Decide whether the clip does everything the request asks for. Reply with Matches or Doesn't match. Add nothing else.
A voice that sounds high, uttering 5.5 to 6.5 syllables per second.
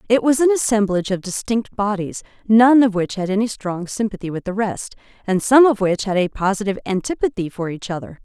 Matches